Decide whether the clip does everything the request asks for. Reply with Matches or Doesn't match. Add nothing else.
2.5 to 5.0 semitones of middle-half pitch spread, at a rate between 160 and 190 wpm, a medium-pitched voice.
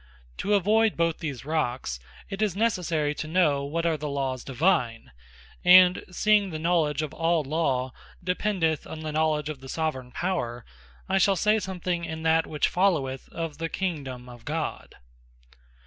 Matches